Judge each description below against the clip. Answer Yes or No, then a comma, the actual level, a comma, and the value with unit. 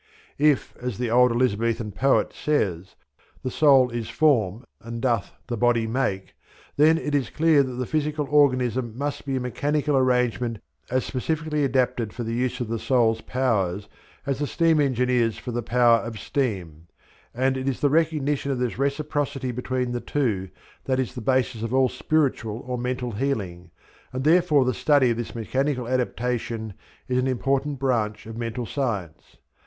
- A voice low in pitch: Yes, low, 125 Hz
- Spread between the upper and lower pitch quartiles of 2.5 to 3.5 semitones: Yes, average, 3.0 semitones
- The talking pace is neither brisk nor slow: Yes, average, 170 wpm